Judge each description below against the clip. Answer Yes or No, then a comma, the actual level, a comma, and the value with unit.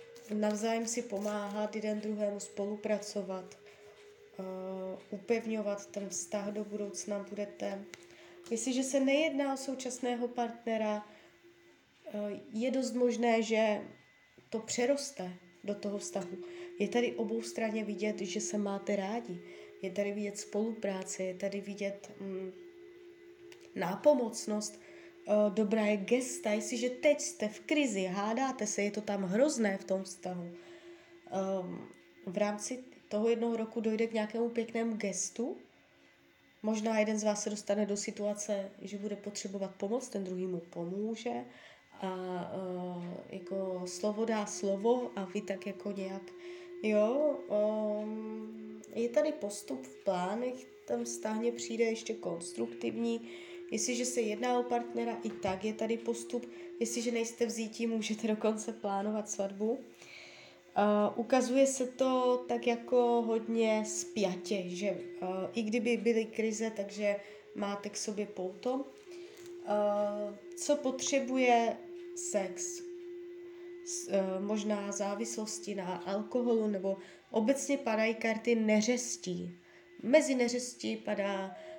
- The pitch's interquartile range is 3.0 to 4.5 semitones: Yes, average, 3.6 semitones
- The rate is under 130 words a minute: Yes, average, 120 wpm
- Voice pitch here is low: No, high, 210 Hz